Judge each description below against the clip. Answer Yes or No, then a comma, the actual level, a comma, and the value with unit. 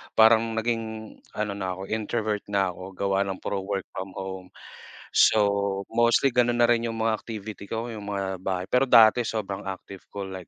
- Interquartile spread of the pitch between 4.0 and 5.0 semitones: No, average, 2.7 semitones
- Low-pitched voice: Yes, low, 105 Hz